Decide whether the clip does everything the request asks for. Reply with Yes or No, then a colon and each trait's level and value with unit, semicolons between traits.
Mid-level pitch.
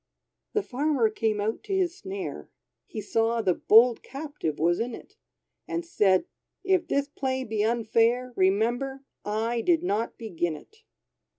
No: high, 235 Hz